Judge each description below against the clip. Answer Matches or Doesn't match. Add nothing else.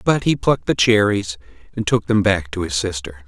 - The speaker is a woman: Doesn't match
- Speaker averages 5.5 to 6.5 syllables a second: Doesn't match